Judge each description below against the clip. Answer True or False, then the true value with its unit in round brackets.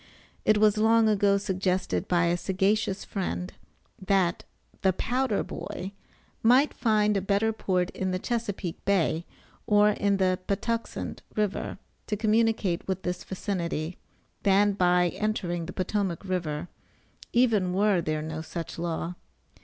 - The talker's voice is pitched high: True (195 Hz)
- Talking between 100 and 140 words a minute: True (135 wpm)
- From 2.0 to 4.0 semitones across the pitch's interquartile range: True (3.0 semitones)